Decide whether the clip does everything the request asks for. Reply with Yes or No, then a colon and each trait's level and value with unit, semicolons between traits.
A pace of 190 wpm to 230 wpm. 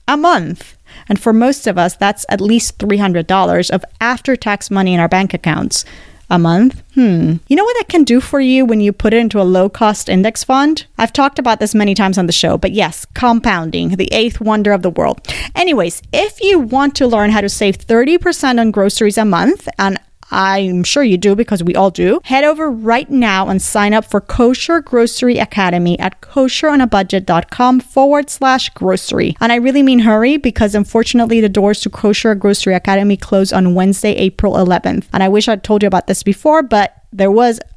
Yes: average, 200 wpm